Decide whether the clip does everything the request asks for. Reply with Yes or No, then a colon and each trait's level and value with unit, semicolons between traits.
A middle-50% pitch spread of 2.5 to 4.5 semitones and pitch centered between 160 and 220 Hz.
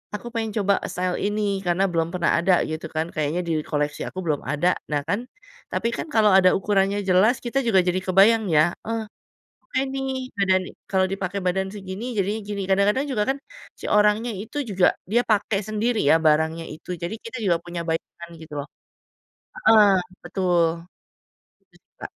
Yes: average, 3.8 semitones; high, 190 Hz